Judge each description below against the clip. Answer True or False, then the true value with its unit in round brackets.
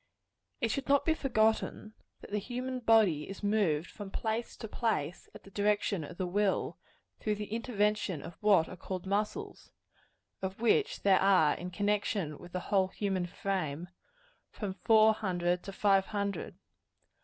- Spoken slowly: False (160 wpm)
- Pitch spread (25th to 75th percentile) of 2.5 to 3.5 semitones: True (3.0 semitones)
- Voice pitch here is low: False (200 Hz)